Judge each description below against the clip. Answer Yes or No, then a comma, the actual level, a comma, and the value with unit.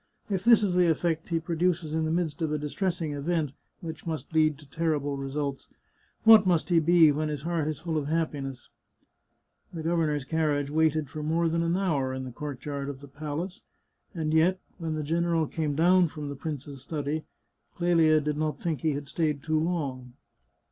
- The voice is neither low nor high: Yes, medium, 155 Hz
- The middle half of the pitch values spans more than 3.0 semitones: No, narrow, 2.5 semitones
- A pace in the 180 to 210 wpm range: Yes, average, 195 wpm